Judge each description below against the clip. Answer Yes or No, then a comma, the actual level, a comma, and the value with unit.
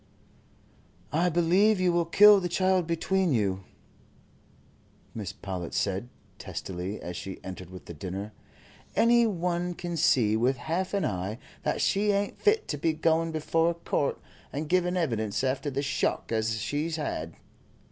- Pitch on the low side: No, medium, 155 Hz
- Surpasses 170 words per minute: No, average, 155 wpm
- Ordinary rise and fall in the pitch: No, wide, 8.8 semitones